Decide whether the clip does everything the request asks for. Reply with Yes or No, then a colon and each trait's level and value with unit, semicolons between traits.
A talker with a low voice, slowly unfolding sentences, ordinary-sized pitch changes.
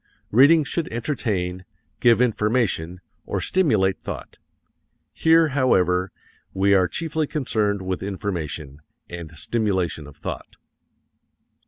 No: low, 100 Hz; slow, 105 wpm; wide, 6.1 semitones